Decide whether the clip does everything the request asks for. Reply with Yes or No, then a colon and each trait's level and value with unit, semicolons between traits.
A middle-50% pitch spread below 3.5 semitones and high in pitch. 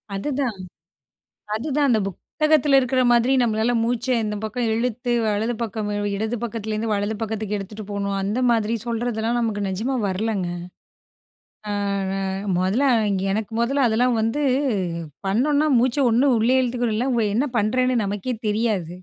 Yes: average, 3.0 semitones; high, 225 Hz